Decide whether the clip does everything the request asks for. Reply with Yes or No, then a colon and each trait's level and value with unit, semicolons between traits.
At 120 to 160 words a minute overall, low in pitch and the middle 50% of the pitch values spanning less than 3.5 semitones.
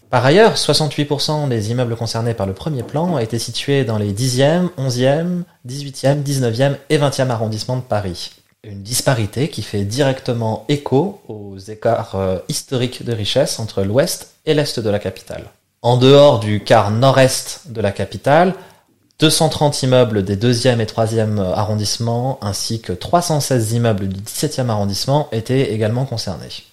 No: average, 150 wpm; low, 125 Hz; average, 4.6 semitones